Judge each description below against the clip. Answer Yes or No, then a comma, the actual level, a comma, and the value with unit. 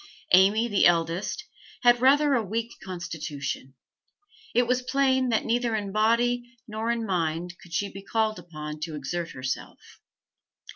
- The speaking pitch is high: Yes, high, 210 Hz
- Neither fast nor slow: Yes, average, 145 wpm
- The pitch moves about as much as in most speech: No, wide, 5.8 semitones